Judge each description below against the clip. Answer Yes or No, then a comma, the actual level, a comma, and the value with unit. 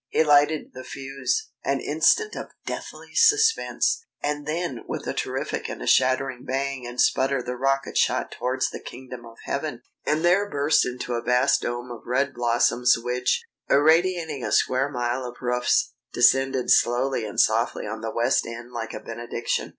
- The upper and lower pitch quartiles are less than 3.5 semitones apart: Yes, average, 2.9 semitones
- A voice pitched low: Yes, low, 130 Hz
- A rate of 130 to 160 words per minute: No, average, 170 wpm